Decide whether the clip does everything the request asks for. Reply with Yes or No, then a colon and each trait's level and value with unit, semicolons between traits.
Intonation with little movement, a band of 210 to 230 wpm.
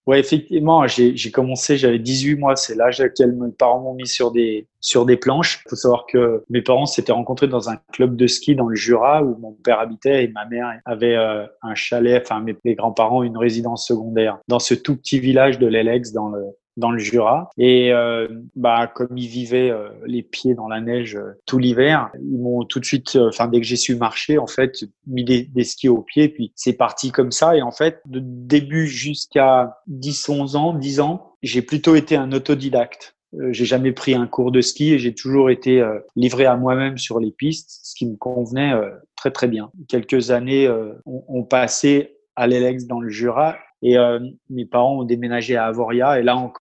Yes: narrow, 2.2 semitones; fast, 220 wpm